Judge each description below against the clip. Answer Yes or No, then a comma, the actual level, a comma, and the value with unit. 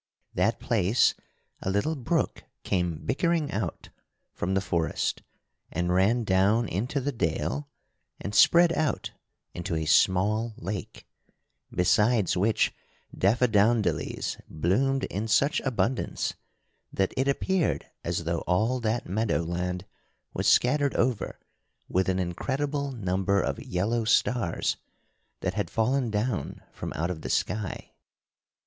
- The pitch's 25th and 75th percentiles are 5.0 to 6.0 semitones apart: Yes, wide, 5.5 semitones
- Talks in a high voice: No, low, 110 Hz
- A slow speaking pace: Yes, slow, 125 wpm